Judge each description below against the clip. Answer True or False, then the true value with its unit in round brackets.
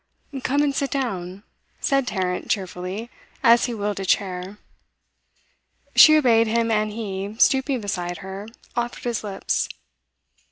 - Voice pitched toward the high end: True (215 Hz)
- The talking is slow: True (130 wpm)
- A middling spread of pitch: True (4.0 semitones)